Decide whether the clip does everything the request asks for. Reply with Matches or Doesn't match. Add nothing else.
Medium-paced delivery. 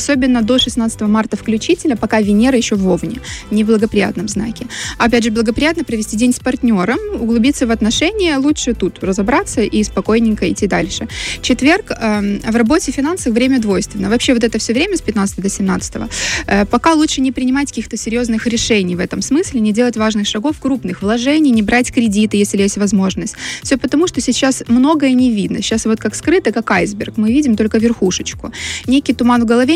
Doesn't match